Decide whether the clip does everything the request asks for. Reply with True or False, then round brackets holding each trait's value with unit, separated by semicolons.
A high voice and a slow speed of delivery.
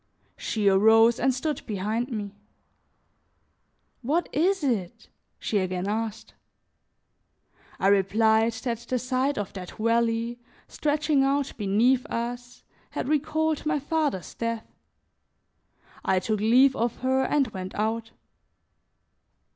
True (235 Hz; 115 wpm)